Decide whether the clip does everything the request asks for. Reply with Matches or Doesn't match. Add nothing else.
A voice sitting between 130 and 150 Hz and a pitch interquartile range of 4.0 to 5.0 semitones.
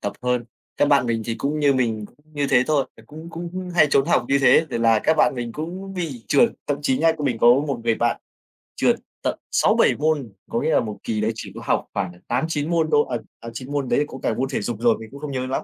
Matches